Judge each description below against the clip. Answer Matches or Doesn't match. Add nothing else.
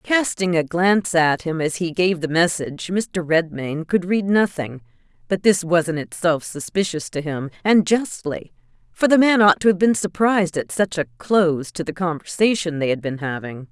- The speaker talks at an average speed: Matches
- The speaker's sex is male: Doesn't match